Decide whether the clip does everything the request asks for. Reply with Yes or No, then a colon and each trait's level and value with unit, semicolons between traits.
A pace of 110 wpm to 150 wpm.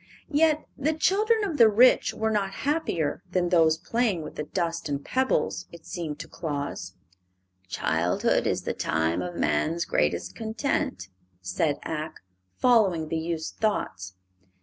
Yes: average, 145 wpm